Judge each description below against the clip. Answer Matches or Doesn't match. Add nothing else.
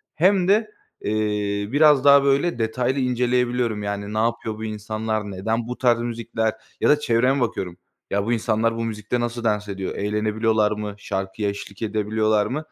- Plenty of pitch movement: Doesn't match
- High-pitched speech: Doesn't match